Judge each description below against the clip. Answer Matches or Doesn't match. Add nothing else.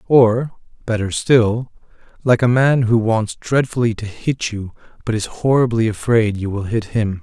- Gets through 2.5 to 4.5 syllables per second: Matches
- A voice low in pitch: Matches